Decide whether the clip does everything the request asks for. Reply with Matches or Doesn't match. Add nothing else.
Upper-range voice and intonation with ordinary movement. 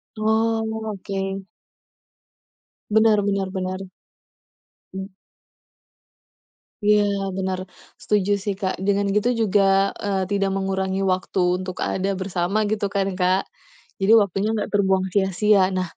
Doesn't match